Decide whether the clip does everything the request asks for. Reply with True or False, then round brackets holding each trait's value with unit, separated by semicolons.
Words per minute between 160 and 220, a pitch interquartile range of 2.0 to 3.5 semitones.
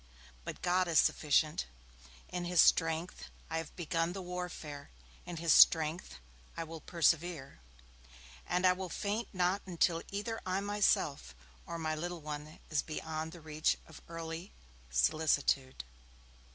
False (140 wpm; 2.5 semitones)